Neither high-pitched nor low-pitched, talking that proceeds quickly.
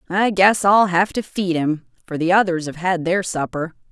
Yes: medium, 180 Hz; fast, 215 wpm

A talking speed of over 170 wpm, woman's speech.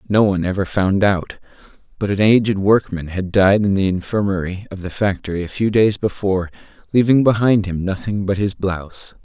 No: average, 180 wpm; male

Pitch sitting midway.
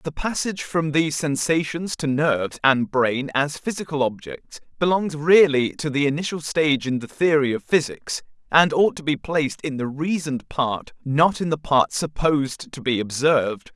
Yes: medium, 150 Hz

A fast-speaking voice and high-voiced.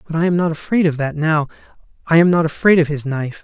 No: fast, 260 wpm; medium, 160 Hz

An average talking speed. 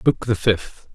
Yes: average, 190 wpm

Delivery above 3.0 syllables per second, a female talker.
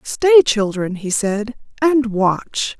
No: 2.9 syllables/s; female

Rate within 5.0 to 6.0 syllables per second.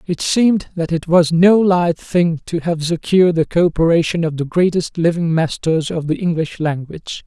No: 4.8 syllables/s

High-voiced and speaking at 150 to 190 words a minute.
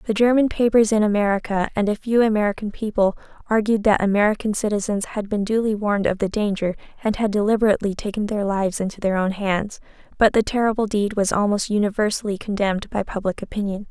Yes: high, 210 Hz; average, 180 wpm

